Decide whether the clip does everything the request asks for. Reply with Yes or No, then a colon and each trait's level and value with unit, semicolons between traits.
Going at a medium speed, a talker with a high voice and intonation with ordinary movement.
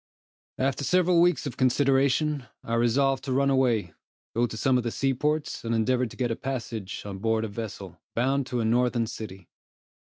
No: average, 185 wpm; low, 125 Hz; average, 3.2 semitones